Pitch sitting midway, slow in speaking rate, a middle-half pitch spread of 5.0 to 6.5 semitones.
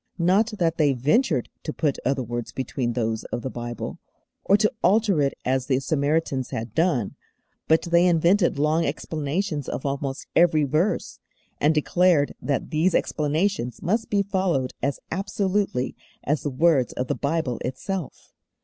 No: medium, 155 Hz; average, 155 wpm; average, 5.3 semitones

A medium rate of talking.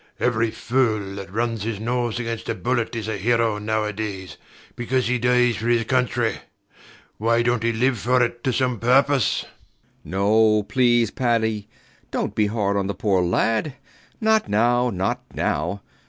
Yes: average, 165 wpm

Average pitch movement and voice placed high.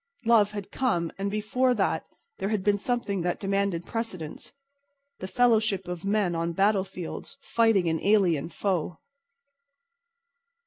Yes: average, 4.0 semitones; high, 200 Hz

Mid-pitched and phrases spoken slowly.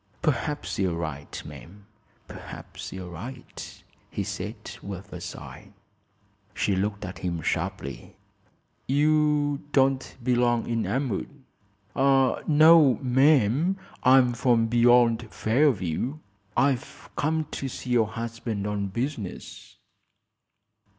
No: low, 120 Hz; slow, 105 wpm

